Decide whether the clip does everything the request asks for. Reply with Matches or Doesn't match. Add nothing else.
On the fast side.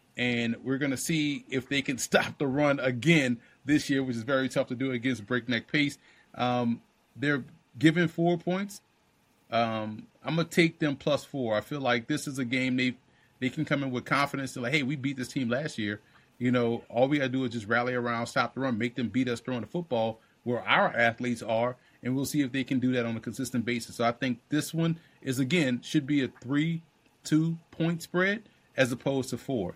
Matches